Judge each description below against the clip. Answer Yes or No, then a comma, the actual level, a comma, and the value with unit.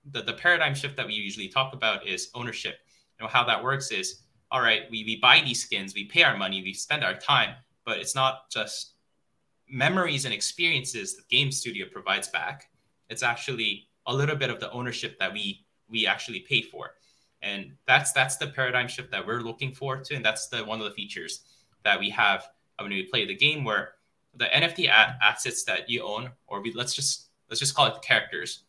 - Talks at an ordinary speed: No, fast, 210 wpm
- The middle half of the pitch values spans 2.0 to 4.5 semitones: Yes, average, 3.6 semitones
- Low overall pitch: Yes, low, 125 Hz